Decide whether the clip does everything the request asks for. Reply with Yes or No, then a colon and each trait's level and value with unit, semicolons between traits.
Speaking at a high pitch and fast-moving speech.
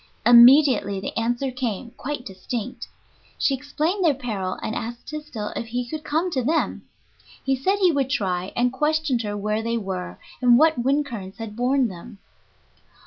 No: high, 245 Hz; average, 170 wpm